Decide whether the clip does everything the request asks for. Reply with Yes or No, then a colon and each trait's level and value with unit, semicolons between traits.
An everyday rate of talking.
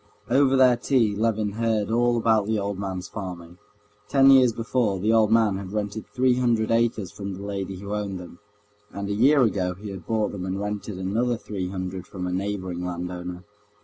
Yes: average, 195 wpm